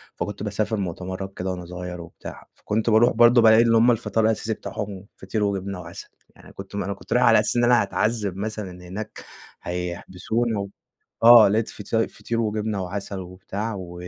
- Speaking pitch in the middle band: No, low, 105 Hz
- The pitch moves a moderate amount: Yes, average, 3.1 semitones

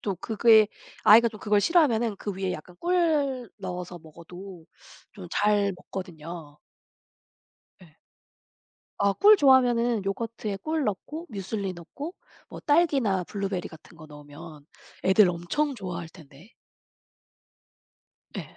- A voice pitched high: Yes, high, 200 Hz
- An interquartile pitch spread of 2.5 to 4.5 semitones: No, average, 5.2 semitones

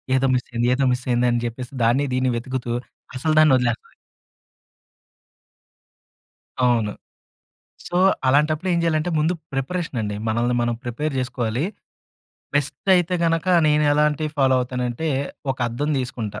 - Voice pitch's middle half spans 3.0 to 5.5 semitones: Yes, average, 4.1 semitones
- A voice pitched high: No, low, 130 Hz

